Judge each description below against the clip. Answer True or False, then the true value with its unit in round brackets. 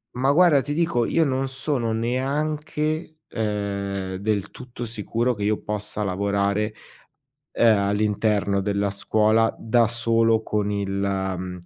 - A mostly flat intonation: False (3.9 semitones)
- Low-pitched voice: True (110 Hz)